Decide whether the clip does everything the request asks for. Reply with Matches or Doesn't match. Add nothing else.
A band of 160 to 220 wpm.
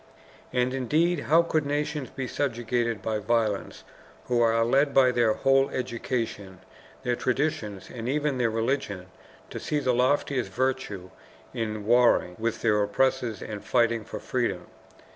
Doesn't match